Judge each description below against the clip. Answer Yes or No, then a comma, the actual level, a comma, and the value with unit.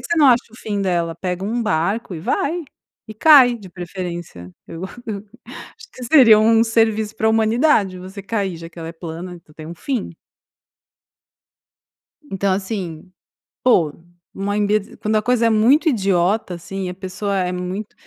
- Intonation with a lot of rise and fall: No, average, 3.9 semitones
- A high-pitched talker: Yes, high, 200 Hz